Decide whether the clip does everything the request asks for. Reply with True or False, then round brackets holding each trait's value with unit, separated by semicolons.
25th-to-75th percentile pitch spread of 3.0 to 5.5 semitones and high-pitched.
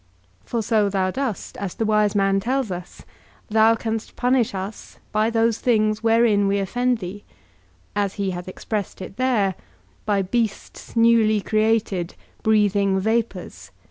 False (2.5 semitones; 215 Hz)